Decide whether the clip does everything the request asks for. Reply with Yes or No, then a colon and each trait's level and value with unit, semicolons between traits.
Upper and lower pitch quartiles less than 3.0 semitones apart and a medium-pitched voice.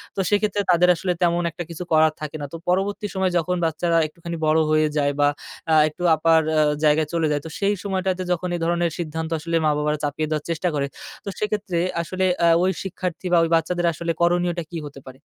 Yes: narrow, 2.6 semitones; medium, 170 Hz